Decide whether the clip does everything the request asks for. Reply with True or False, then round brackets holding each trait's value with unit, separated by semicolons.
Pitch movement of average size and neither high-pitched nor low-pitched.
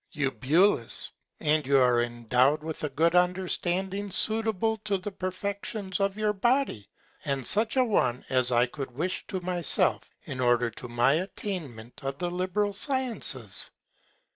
False (7.6 semitones; 175 Hz)